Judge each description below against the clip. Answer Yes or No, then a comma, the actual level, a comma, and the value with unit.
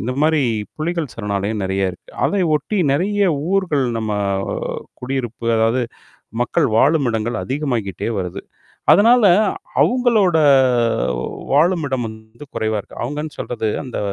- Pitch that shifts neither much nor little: No, wide, 6.9 semitones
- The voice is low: Yes, low, 130 Hz